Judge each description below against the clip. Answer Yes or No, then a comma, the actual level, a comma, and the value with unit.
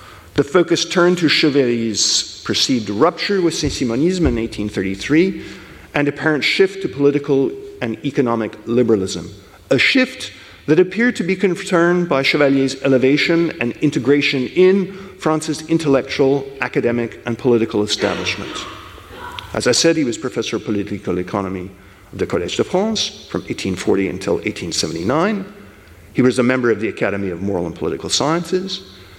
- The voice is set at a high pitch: No, low, 135 Hz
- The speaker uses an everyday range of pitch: No, wide, 7.6 semitones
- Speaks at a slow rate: Yes, slow, 140 wpm